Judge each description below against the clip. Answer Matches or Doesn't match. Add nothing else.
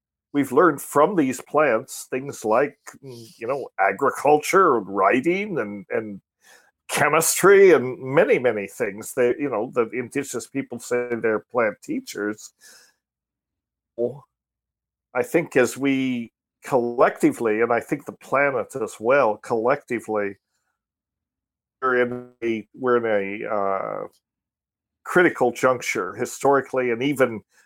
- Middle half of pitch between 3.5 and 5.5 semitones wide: Matches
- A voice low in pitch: Matches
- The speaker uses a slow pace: Matches